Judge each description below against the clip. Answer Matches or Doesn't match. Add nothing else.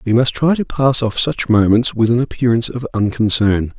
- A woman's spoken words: Doesn't match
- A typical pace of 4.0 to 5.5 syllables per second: Matches